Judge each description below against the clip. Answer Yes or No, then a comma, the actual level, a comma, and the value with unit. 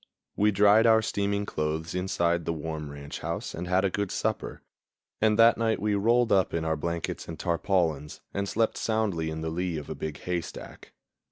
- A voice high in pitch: No, very low, 90 Hz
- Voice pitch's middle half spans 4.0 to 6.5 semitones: Yes, average, 4.3 semitones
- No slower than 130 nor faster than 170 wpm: No, average, 190 wpm